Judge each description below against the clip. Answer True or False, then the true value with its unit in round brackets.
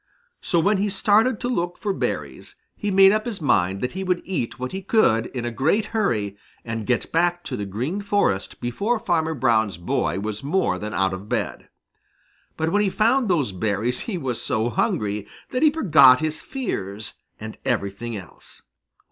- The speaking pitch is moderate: True (145 Hz)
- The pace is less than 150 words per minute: False (185 wpm)